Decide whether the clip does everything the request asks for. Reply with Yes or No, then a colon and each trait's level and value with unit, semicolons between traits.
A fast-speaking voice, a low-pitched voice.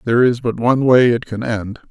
Yes: fast, 250 wpm; low, 120 Hz